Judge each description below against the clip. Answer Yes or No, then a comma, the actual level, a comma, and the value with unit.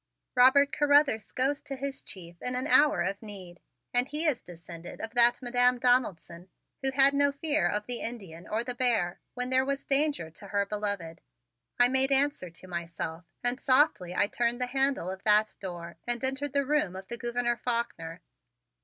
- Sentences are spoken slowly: No, average, 185 wpm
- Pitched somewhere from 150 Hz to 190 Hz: No, high, 240 Hz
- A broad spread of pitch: Yes, wide, 6.0 semitones